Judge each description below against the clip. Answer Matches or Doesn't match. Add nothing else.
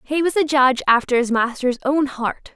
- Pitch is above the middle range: Matches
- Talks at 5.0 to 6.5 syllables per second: Matches